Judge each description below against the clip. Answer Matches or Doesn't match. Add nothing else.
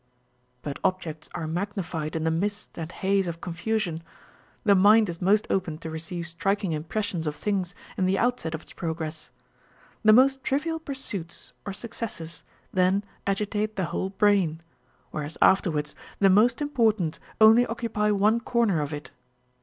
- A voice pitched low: Doesn't match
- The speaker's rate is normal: Matches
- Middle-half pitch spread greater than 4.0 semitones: Matches